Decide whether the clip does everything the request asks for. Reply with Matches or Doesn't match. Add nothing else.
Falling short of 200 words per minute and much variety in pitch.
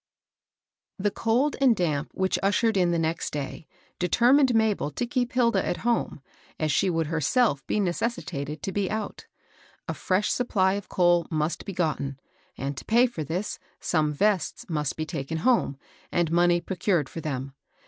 Matches